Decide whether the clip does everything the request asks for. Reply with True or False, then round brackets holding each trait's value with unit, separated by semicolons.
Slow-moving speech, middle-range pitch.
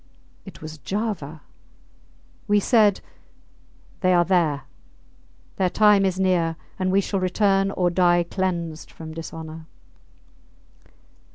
True (110 wpm; 180 Hz)